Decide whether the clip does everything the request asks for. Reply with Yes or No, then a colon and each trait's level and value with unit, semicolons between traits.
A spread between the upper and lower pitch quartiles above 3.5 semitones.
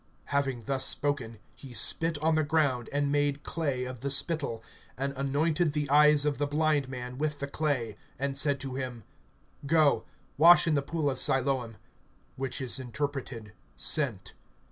No: narrow, 2.5 semitones